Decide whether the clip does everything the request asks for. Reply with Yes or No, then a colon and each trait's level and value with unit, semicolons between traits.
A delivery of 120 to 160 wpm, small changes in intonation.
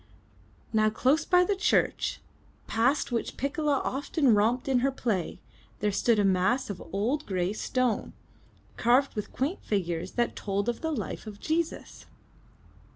No: average, 150 wpm; average, 5.3 semitones